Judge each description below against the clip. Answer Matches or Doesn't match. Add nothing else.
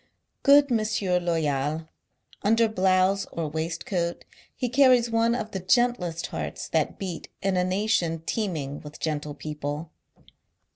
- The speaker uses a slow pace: Matches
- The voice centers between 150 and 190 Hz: Matches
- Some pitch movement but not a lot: Doesn't match